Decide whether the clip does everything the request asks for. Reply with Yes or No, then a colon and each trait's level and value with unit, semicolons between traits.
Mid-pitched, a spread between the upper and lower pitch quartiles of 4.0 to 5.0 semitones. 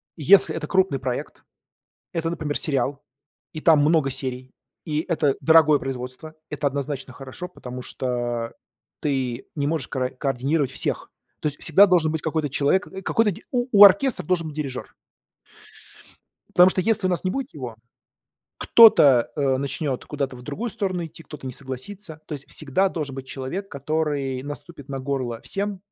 Yes: medium, 150 Hz; average, 4.5 semitones